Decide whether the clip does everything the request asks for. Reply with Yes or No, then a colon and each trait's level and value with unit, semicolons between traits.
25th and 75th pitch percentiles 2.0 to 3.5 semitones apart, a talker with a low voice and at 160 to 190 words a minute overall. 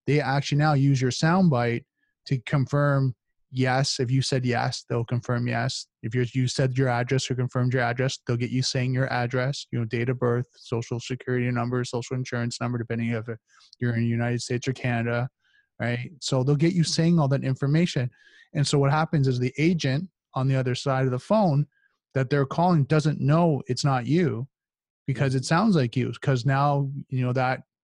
No: narrow, 2.6 semitones; low, 130 Hz; average, 200 wpm